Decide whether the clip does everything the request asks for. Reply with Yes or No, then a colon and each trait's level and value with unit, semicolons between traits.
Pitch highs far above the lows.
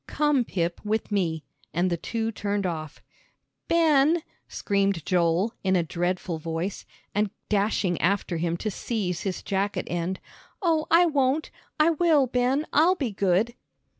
Yes: wide, 7.3 semitones